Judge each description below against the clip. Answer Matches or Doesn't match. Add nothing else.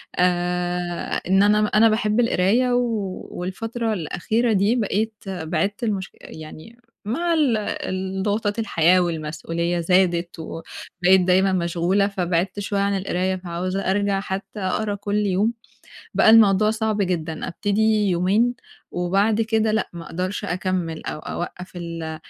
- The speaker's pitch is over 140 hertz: Matches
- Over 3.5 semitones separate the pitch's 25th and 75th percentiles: Doesn't match